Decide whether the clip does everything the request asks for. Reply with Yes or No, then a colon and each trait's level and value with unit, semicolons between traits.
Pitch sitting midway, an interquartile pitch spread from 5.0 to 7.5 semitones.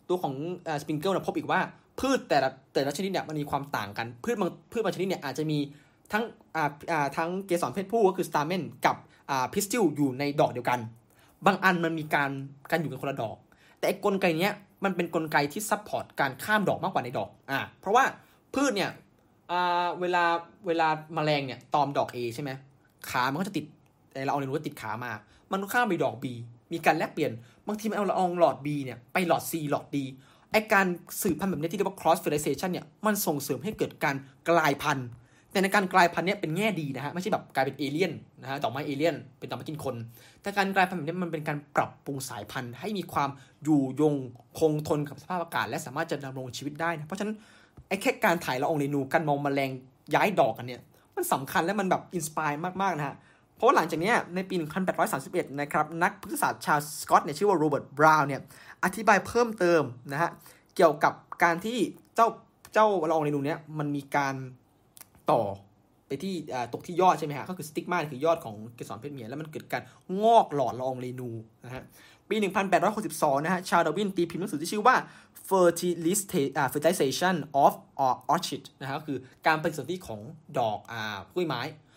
No: medium, 155 Hz; average, 4.6 semitones